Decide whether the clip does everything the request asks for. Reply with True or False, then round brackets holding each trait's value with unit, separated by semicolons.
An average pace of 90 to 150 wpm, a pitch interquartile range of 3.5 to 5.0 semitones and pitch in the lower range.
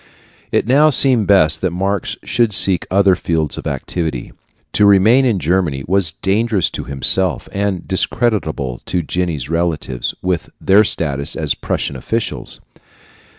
True (140 wpm; 4.4 semitones; 95 Hz)